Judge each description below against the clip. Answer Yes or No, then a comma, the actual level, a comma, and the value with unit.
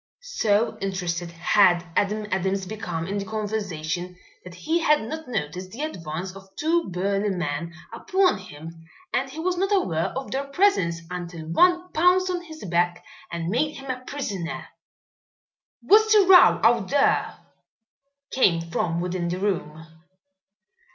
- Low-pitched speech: No, high, 195 Hz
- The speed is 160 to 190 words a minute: No, average, 145 wpm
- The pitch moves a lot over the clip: Yes, wide, 9.0 semitones